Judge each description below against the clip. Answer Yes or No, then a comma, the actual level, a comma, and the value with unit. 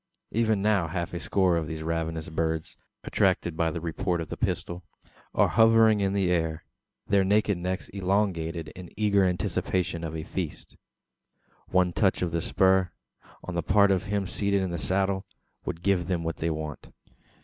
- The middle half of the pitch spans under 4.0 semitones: Yes, average, 3.0 semitones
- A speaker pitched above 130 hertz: No, very low, 90 Hz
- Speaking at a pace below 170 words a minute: No, average, 175 wpm